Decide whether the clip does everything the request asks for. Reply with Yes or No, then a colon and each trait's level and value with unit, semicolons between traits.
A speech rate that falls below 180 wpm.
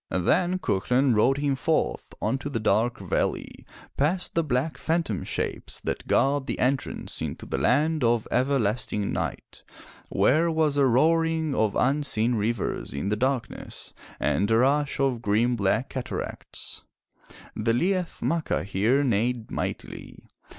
Yes: average, 140 wpm